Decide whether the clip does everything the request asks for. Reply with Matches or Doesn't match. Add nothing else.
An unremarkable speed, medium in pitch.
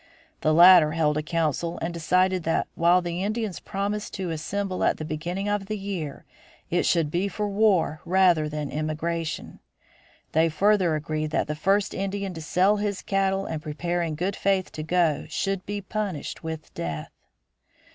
Matches